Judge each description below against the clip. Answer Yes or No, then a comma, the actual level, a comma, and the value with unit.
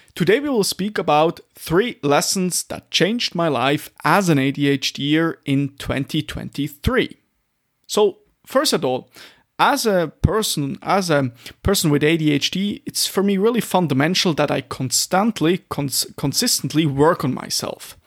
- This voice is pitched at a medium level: Yes, medium, 155 Hz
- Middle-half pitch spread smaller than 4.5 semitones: No, average, 5.2 semitones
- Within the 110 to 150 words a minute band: Yes, slow, 135 wpm